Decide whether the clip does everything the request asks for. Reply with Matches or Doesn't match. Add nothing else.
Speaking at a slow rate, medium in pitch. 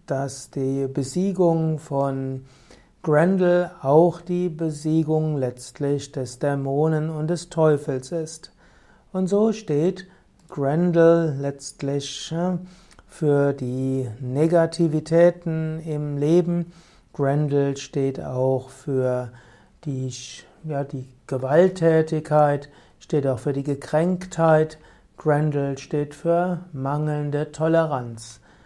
Matches